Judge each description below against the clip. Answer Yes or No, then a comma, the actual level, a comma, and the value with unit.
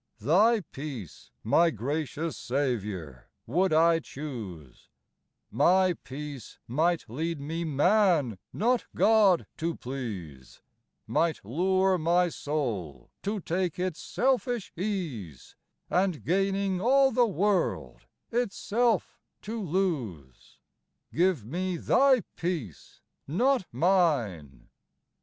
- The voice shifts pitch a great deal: Yes, wide, 7.3 semitones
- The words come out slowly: Yes, slow, 100 wpm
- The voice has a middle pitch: Yes, medium, 165 Hz